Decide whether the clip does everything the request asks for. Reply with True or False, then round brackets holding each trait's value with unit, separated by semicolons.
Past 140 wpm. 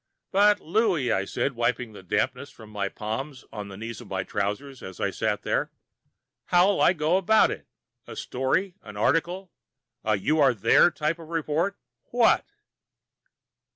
True (160 wpm)